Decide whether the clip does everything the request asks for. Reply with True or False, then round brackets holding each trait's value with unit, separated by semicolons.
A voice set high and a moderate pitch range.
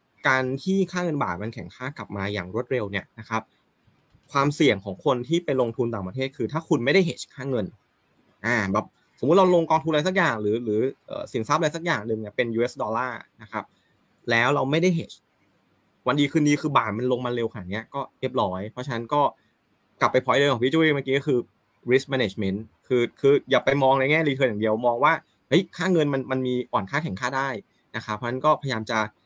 False (130 Hz; 4.8 semitones)